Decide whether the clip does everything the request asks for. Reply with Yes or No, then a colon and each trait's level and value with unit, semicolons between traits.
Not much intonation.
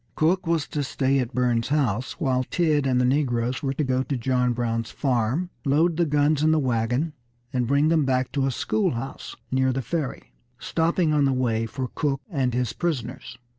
No: average, 3.3 semitones